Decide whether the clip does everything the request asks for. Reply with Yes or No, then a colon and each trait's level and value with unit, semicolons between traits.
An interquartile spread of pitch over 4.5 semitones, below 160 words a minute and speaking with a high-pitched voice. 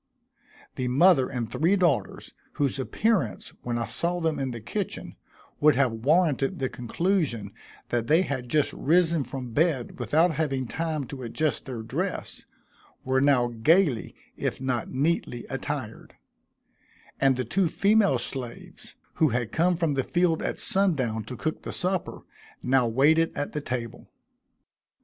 No: average, 5.0 semitones; average, 150 wpm; low, 135 Hz